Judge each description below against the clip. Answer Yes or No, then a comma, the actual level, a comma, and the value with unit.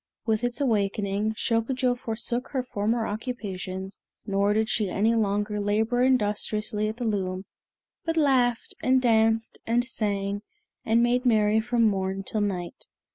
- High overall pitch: Yes, high, 220 Hz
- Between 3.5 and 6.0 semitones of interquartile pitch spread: No, average, 2.9 semitones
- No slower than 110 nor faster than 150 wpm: Yes, average, 140 wpm